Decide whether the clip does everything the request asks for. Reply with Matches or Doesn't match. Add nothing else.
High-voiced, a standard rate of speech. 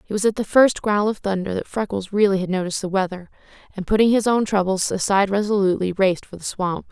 Doesn't match